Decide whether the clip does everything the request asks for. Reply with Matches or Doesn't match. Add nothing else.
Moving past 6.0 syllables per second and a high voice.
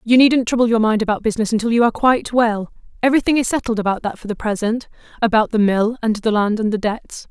Matches